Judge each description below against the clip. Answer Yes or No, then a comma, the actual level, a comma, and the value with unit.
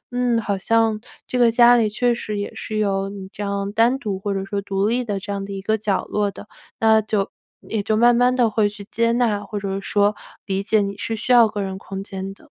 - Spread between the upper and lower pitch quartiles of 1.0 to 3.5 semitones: Yes, narrow, 2.5 semitones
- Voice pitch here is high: Yes, high, 210 Hz